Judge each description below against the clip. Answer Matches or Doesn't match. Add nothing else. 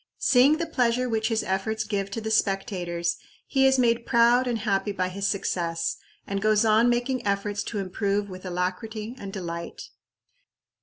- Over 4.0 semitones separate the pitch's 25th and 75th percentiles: Doesn't match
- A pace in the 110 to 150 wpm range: Doesn't match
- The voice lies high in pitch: Matches